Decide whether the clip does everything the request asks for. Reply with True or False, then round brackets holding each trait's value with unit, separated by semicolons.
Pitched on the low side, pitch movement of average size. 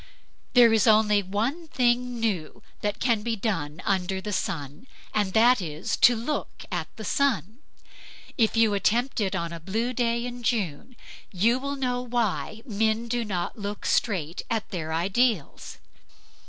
False (220 Hz; 4.1 semitones)